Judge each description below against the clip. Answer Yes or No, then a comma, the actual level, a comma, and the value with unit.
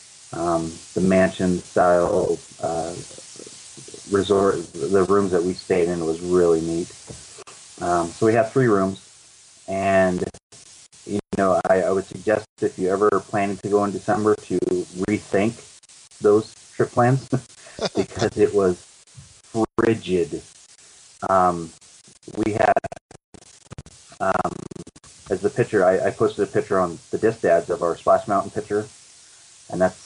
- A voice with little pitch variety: No, average, 3.2 semitones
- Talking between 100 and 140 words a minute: Yes, slow, 135 wpm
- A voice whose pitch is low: Yes, very low, 95 Hz